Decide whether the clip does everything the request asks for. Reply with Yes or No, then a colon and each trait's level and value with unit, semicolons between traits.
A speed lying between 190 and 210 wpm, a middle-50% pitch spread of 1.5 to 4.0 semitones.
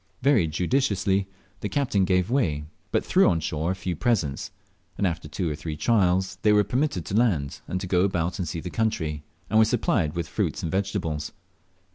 No: average, 195 wpm; average, 4.4 semitones